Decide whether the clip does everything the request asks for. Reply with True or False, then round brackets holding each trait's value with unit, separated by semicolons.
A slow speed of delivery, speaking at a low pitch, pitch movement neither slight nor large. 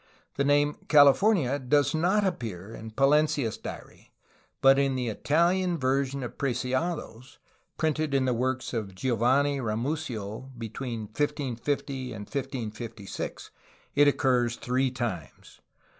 True (120 wpm; 130 Hz; 3.6 semitones)